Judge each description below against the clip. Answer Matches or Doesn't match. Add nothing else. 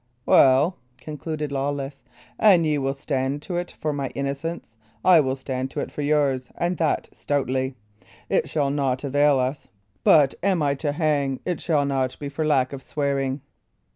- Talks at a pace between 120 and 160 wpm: Doesn't match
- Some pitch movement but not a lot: Doesn't match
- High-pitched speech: Doesn't match